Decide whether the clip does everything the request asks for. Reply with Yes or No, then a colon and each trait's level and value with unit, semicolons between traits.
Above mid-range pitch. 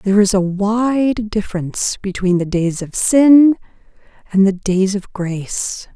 Yes: high, 200 Hz